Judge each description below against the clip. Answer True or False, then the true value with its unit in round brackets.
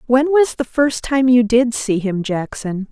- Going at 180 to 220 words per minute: True (205 wpm)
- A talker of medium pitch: False (240 Hz)